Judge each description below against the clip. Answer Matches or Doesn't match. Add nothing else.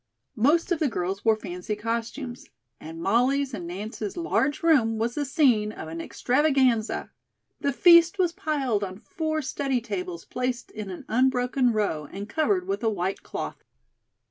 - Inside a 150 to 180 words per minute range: Matches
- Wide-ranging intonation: Matches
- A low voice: Doesn't match